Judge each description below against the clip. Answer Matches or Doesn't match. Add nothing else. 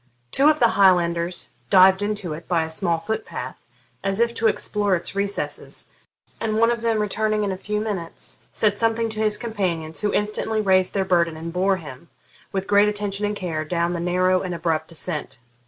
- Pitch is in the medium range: Doesn't match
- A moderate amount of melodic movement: Matches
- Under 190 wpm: Doesn't match